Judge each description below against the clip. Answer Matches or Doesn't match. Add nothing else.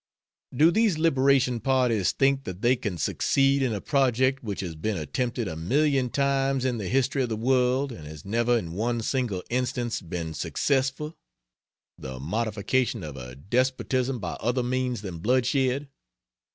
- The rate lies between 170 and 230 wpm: Doesn't match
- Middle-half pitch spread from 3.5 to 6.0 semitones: Matches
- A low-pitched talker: Matches